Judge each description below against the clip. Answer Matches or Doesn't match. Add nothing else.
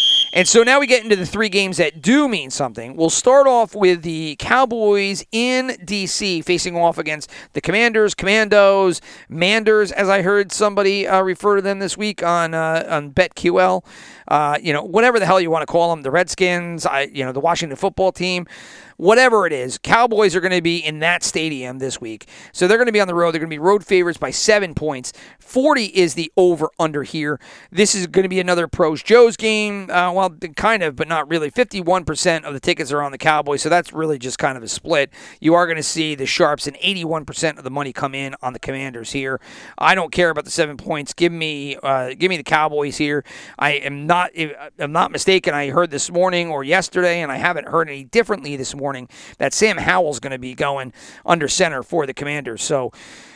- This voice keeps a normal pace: Doesn't match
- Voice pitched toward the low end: Doesn't match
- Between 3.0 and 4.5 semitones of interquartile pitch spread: Doesn't match